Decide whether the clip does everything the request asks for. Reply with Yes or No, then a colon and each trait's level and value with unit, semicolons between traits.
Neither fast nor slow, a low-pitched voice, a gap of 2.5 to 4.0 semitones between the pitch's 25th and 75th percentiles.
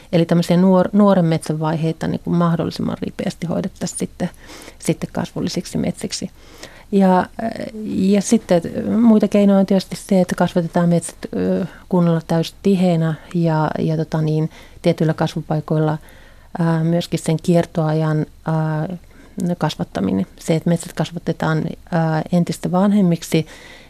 No: average, 115 wpm; medium, 170 Hz; average, 2.9 semitones